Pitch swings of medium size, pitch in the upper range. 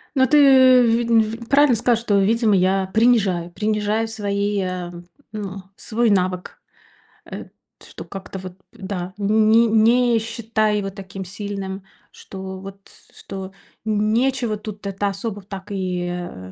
Yes: average, 3.0 semitones; high, 205 Hz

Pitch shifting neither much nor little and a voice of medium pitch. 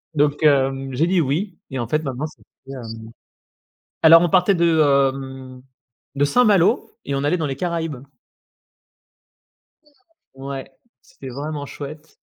Yes: average, 3.5 semitones; medium, 145 Hz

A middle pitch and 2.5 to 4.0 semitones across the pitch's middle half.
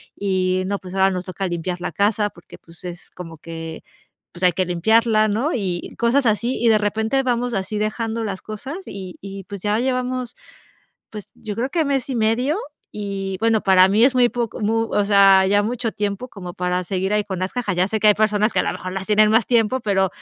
No: high, 205 Hz; average, 3.3 semitones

